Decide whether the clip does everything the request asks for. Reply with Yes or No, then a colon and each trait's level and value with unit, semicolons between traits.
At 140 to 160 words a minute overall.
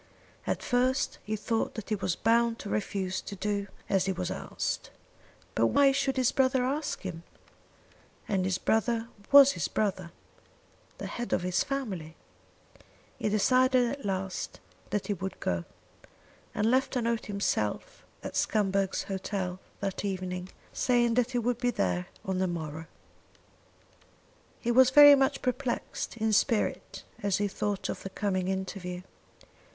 Yes: average, 150 wpm